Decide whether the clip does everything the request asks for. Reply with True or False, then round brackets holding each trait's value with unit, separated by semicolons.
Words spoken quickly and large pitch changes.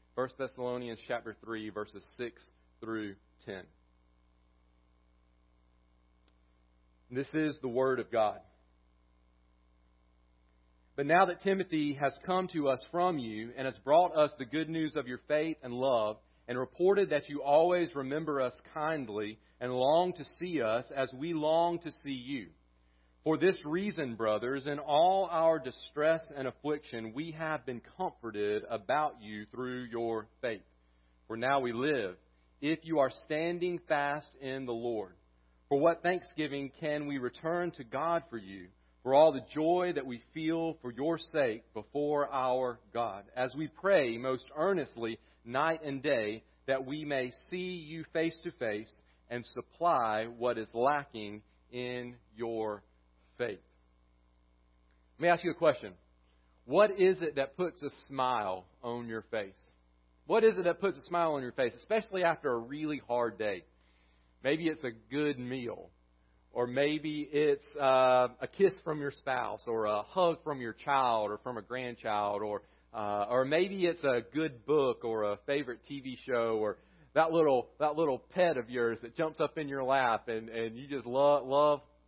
False (165 wpm; 6.4 semitones)